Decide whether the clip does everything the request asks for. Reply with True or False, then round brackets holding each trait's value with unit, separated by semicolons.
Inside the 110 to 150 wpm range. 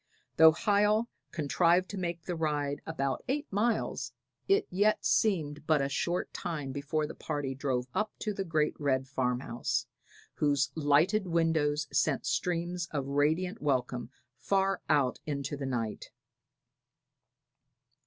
True (135 wpm)